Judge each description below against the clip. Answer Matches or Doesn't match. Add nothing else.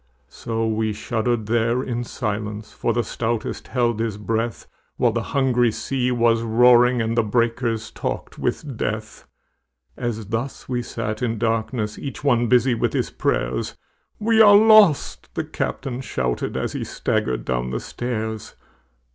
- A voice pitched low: Matches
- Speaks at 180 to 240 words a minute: Doesn't match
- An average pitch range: Doesn't match